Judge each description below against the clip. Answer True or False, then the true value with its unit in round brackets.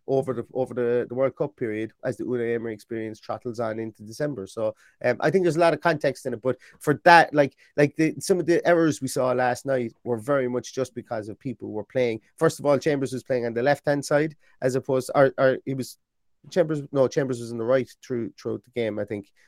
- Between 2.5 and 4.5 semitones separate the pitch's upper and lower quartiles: True (3.6 semitones)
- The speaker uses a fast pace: True (255 wpm)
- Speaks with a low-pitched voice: True (130 Hz)